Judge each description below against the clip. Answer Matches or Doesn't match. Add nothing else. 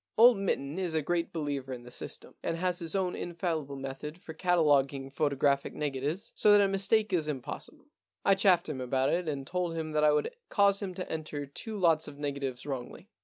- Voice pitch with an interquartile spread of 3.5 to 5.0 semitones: Matches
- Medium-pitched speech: Matches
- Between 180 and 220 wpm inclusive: Matches